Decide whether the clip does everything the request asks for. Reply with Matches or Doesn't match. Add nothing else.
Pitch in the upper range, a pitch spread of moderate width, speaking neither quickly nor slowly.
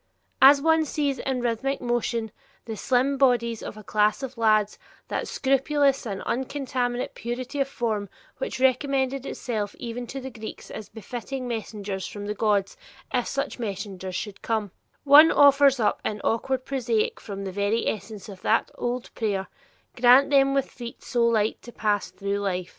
Matches